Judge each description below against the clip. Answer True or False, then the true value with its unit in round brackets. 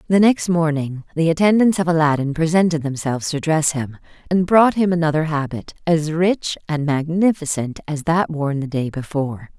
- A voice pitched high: False (160 Hz)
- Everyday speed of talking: True (170 wpm)